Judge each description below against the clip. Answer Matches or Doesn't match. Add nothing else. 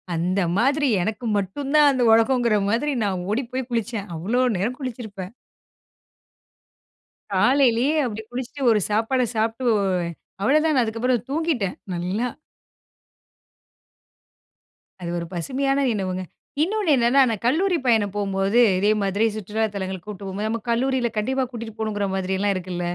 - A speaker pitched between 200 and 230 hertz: Matches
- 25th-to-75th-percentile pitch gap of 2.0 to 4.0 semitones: Doesn't match